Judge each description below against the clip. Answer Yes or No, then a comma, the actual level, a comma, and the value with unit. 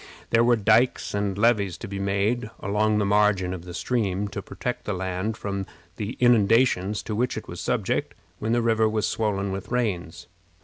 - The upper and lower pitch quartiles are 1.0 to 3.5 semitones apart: Yes, narrow, 2.6 semitones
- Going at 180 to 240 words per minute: Yes, average, 185 wpm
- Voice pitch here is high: No, low, 105 Hz